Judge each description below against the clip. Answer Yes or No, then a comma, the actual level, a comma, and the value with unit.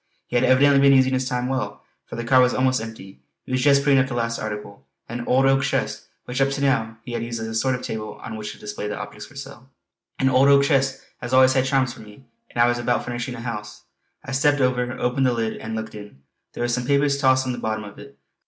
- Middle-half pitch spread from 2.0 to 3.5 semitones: Yes, average, 3.0 semitones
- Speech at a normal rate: No, fast, 265 wpm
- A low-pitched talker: Yes, low, 125 Hz